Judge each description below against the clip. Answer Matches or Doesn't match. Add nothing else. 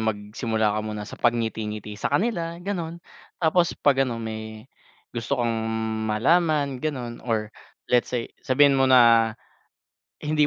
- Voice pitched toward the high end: Doesn't match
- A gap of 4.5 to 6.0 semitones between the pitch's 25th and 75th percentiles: Matches